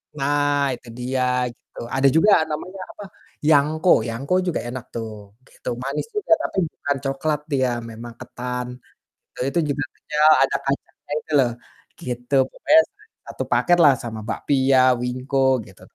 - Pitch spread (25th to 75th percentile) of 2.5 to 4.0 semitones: Yes, average, 3.2 semitones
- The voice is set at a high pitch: No, low, 135 Hz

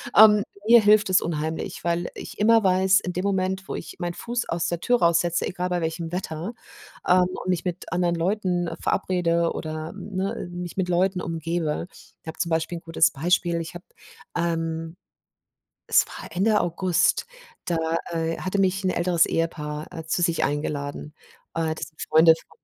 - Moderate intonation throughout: No, narrow, 2.2 semitones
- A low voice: No, medium, 175 Hz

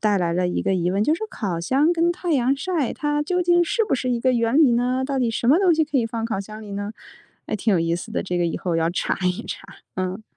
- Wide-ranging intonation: Yes, wide, 7.5 semitones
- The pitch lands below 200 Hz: No, high, 235 Hz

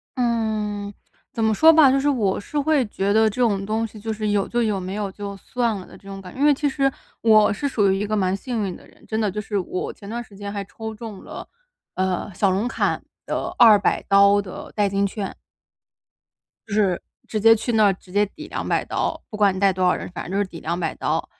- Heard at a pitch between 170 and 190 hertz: No, high, 210 Hz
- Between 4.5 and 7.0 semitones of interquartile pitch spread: No, narrow, 2.5 semitones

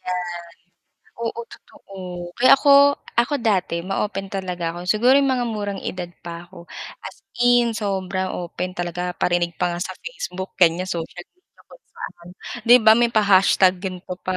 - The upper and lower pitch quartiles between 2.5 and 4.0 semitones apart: No, average, 4.7 semitones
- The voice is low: No, high, 190 Hz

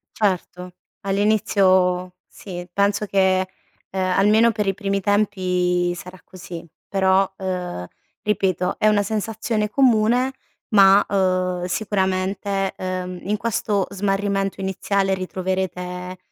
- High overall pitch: Yes, high, 195 Hz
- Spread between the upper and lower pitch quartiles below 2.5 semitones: Yes, narrow, 1.9 semitones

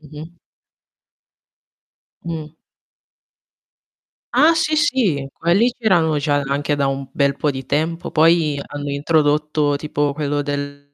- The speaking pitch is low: No, medium, 150 Hz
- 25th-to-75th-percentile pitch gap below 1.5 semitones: No, narrow, 2.6 semitones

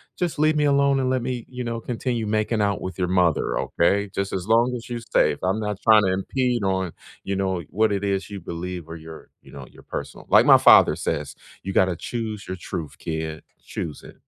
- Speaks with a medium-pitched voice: No, low, 100 Hz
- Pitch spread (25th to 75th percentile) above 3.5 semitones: Yes, average, 4.6 semitones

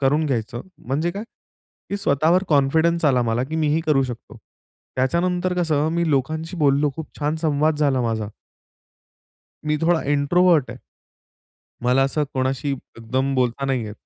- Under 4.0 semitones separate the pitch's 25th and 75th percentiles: Yes, average, 3.5 semitones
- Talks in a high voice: No, medium, 145 Hz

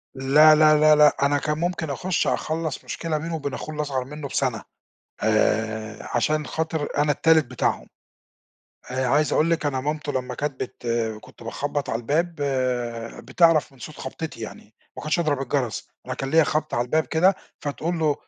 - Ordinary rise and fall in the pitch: Yes, average, 3.1 semitones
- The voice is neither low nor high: Yes, medium, 150 Hz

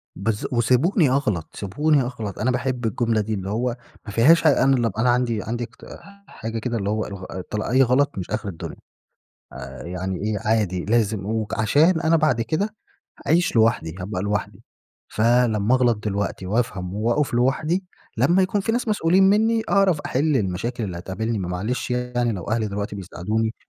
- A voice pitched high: No, low, 115 Hz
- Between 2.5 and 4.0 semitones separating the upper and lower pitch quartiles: No, average, 4.4 semitones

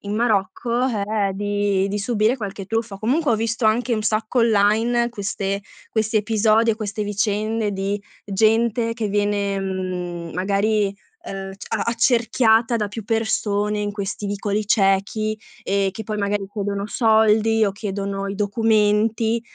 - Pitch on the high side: Yes, high, 210 Hz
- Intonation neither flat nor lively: No, narrow, 2.0 semitones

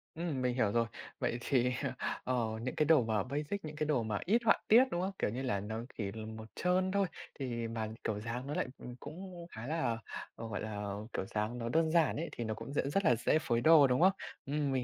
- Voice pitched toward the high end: No, low, 125 Hz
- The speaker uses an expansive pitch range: Yes, wide, 5.9 semitones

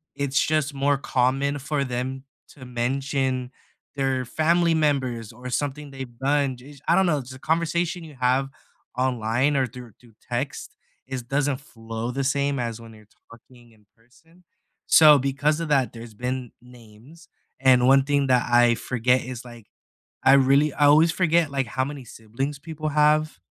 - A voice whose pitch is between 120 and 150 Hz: Yes, low, 135 Hz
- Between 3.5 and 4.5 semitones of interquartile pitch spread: No, average, 2.9 semitones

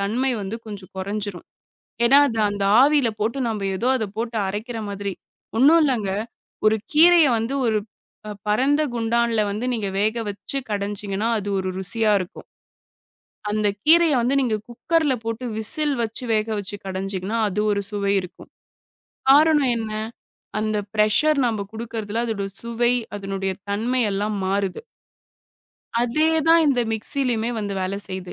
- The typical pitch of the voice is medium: No, high, 220 Hz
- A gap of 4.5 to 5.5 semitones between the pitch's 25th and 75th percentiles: No, average, 3.5 semitones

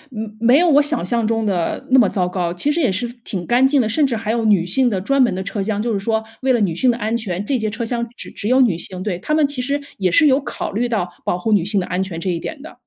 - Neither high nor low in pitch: No, high, 220 Hz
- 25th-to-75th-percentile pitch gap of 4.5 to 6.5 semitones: Yes, average, 4.9 semitones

